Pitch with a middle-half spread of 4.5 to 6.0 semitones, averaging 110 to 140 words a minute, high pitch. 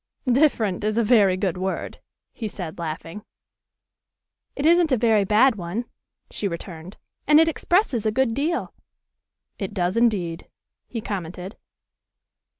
Yes: wide, 5.4 semitones; slow, 135 wpm; high, 210 Hz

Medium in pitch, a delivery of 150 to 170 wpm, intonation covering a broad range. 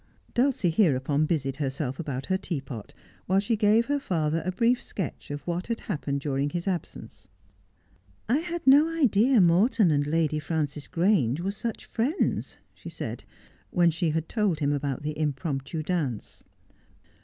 Yes: medium, 165 Hz; average, 160 wpm; wide, 6.4 semitones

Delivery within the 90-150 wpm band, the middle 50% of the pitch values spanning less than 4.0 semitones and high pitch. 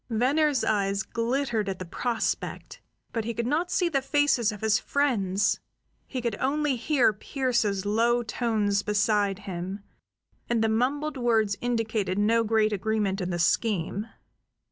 Yes: average, 145 wpm; average, 3.5 semitones; high, 225 Hz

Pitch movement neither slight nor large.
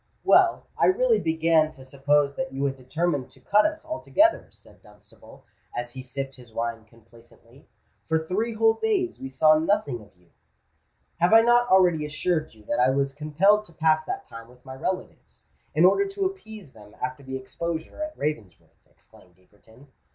No: wide, 7.5 semitones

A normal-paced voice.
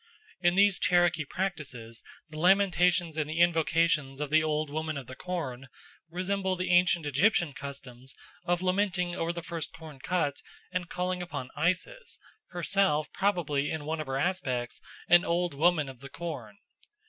Yes: average, 160 wpm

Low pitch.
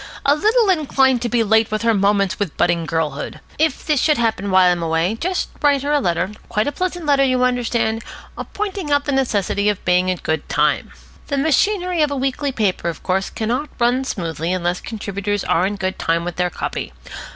No: high, 225 Hz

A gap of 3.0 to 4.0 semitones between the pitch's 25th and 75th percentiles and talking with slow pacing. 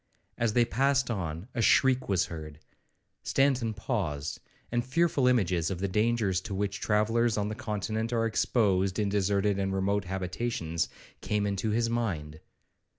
No: average, 3.6 semitones; average, 155 wpm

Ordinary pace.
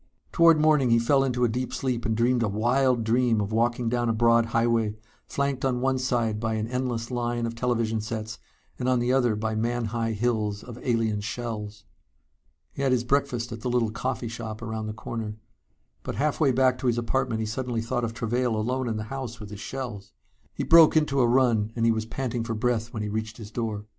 No: fast, 220 wpm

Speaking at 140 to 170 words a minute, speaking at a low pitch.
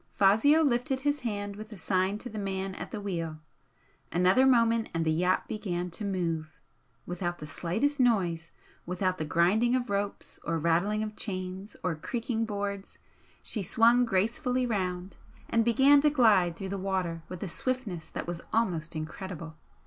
No: average, 165 wpm; high, 195 Hz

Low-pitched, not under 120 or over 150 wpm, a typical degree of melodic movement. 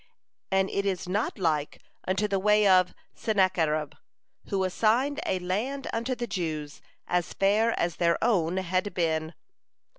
No: high, 190 Hz; average, 145 wpm; average, 3.6 semitones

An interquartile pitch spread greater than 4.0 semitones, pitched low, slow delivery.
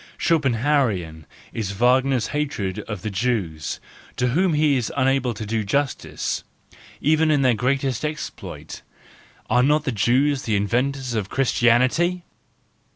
Yes: average, 4.5 semitones; low, 125 Hz; slow, 130 wpm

